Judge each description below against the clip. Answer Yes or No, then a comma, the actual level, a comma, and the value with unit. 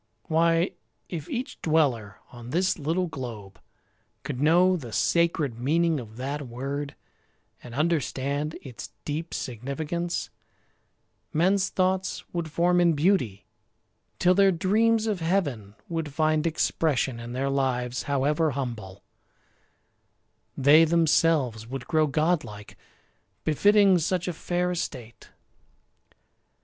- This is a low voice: No, medium, 155 Hz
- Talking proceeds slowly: Yes, slow, 115 wpm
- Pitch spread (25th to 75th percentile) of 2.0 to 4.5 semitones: No, average, 5.0 semitones